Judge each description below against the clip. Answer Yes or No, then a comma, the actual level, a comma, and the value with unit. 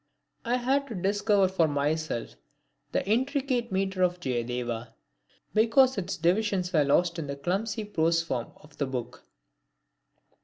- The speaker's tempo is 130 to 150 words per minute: Yes, average, 140 wpm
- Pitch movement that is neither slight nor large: No, wide, 6.9 semitones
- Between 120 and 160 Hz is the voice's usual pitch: No, medium, 180 Hz